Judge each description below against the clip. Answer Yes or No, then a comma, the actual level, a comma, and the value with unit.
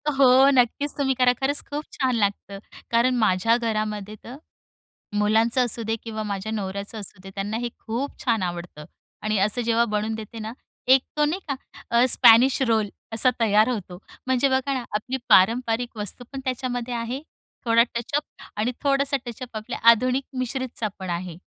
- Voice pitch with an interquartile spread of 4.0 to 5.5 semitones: No, average, 3.3 semitones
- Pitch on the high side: Yes, high, 230 Hz